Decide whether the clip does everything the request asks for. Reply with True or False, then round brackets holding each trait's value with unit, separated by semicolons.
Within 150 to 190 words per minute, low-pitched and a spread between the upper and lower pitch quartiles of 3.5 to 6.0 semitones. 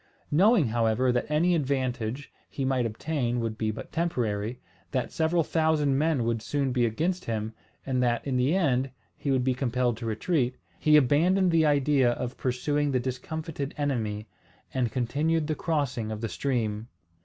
True (165 wpm; 130 Hz; 4.2 semitones)